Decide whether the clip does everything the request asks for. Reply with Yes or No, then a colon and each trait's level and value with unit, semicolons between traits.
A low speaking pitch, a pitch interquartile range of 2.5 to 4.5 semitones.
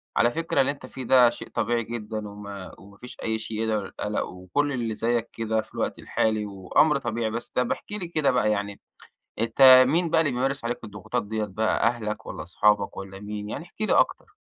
Yes: low, 115 Hz; average, 3.6 semitones